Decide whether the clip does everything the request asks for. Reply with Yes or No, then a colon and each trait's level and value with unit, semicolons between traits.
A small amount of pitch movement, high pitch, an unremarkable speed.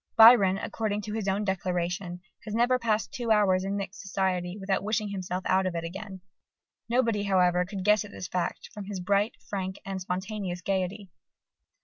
Yes: narrow, 2.3 semitones; high, 195 Hz; average, 175 wpm